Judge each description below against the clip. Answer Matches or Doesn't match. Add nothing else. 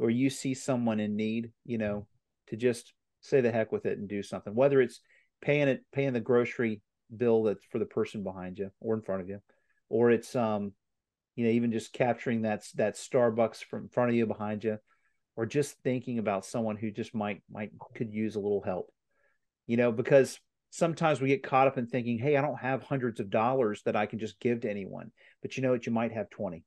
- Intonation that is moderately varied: Matches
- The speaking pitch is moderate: Doesn't match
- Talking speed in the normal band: Doesn't match